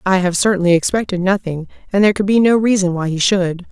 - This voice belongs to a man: No, female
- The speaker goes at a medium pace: No, fast, 225 wpm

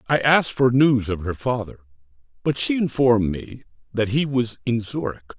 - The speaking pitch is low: Yes, low, 120 Hz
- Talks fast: No, average, 180 wpm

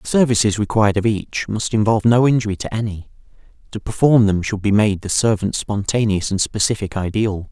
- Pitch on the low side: Yes, low, 105 Hz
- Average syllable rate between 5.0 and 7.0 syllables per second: Yes, 5.7 syllables/s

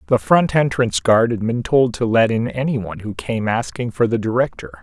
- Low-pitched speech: Yes, low, 110 Hz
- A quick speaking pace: Yes, fast, 210 wpm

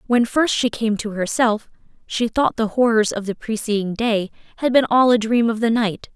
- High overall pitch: Yes, high, 225 Hz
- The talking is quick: Yes, fast, 215 wpm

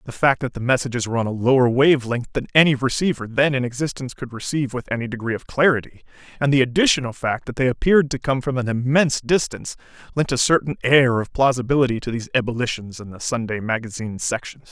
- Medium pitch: No, low, 130 Hz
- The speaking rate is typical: No, fast, 210 wpm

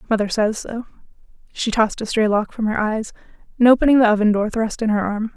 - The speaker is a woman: Yes, female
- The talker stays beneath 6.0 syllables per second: No, 6.2 syllables/s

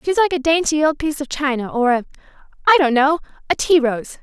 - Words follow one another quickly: Yes, fast, 215 wpm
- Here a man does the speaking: No, female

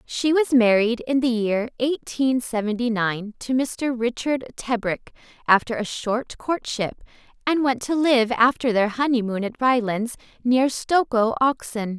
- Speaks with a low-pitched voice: No, high, 240 Hz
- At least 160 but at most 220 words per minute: No, average, 145 wpm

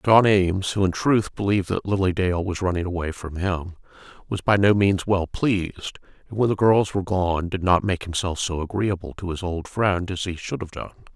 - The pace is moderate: No, fast, 220 wpm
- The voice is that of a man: Yes, male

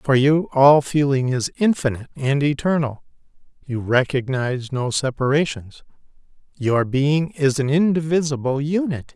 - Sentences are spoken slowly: Yes, slow, 120 wpm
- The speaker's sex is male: Yes, male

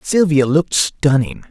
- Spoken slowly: Yes, slow, 120 wpm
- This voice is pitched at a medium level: Yes, medium, 150 Hz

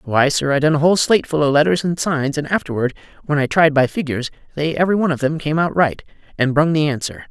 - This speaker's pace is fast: Yes, fast, 255 wpm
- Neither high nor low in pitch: Yes, medium, 150 Hz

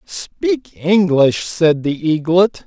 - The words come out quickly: No, slow, 115 wpm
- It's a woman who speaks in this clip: No, male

